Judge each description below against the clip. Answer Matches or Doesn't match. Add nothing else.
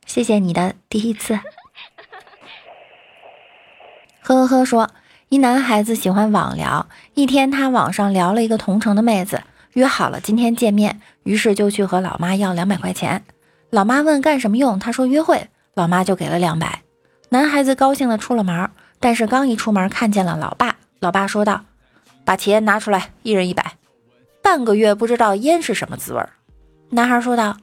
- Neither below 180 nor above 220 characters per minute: Doesn't match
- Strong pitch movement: Doesn't match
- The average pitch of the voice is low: Doesn't match